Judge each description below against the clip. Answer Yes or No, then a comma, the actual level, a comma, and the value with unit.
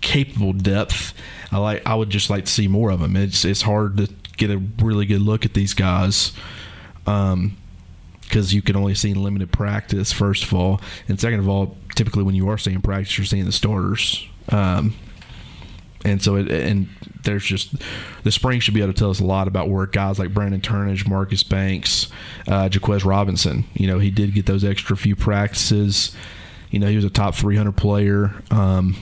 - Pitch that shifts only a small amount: Yes, narrow, 1.4 semitones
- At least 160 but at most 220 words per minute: Yes, average, 200 wpm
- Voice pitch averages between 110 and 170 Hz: No, low, 100 Hz